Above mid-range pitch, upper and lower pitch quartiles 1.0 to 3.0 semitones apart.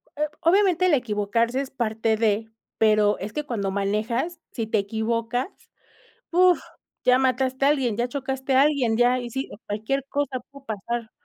No: high, 245 Hz; average, 3.8 semitones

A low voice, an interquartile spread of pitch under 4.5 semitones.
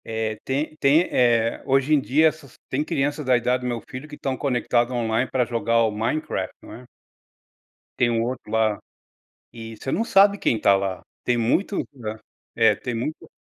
Yes: low, 125 Hz; average, 3.5 semitones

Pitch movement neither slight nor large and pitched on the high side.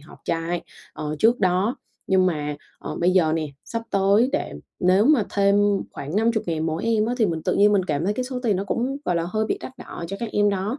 Yes: average, 4.9 semitones; high, 195 Hz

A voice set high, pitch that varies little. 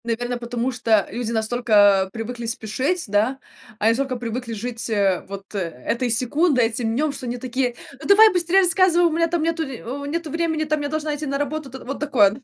No: very high, 250 Hz; average, 5.3 semitones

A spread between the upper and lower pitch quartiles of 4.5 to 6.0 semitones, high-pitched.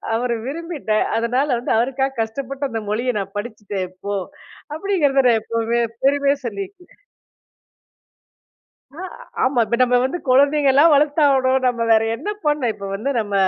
No: average, 3.9 semitones; very high, 255 Hz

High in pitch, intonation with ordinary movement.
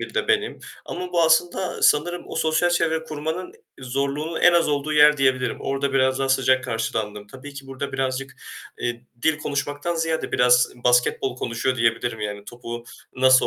No: low, 135 Hz; average, 4.2 semitones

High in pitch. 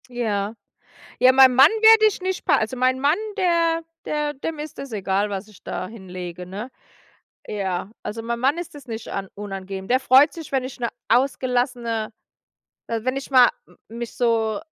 Yes: high, 245 Hz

